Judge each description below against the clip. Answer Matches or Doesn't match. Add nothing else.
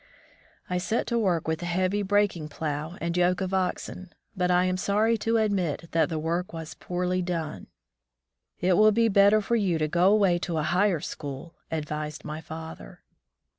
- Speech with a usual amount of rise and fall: Matches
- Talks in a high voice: Doesn't match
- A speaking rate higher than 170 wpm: Matches